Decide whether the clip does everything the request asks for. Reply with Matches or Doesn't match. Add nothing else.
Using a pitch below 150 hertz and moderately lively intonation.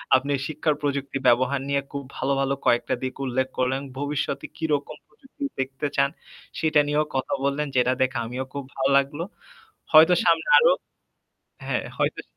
Doesn't match